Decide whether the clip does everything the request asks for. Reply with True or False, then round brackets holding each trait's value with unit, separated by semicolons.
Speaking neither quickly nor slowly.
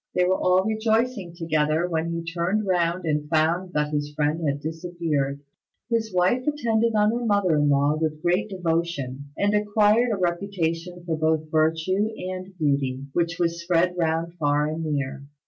True (165 wpm)